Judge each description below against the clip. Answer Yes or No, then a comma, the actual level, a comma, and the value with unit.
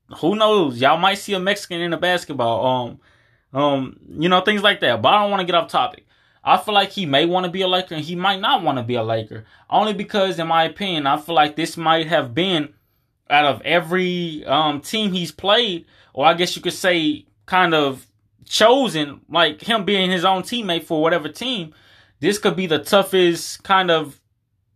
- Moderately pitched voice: Yes, medium, 165 Hz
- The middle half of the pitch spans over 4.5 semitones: Yes, average, 5.1 semitones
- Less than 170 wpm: No, fast, 205 wpm